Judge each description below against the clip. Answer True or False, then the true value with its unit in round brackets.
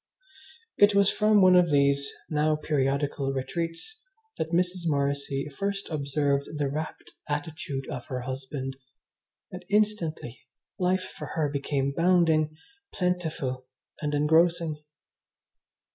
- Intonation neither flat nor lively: True (4.1 semitones)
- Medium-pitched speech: True (155 Hz)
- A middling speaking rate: False (115 wpm)